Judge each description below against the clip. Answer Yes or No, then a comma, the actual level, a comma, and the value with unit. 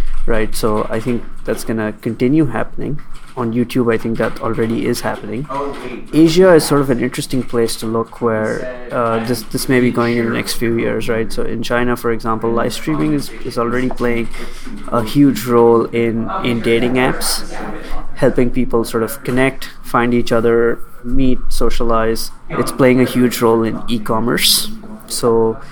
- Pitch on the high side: No, low, 120 Hz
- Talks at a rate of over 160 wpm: Yes, average, 175 wpm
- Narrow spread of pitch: Yes, narrow, 1.9 semitones